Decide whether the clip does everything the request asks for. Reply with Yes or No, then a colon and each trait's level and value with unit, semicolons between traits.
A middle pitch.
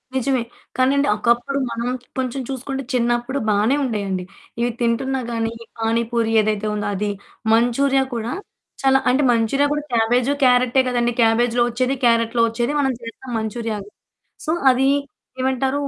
No: high, 240 Hz